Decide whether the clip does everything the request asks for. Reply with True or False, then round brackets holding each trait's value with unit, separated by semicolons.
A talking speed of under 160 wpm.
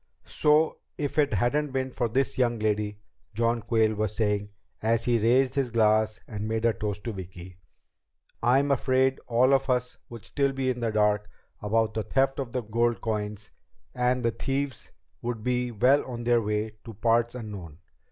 False (180 wpm)